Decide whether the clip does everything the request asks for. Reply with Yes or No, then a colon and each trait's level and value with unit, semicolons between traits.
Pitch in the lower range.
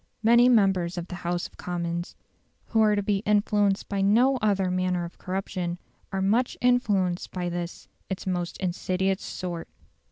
No: high, 190 Hz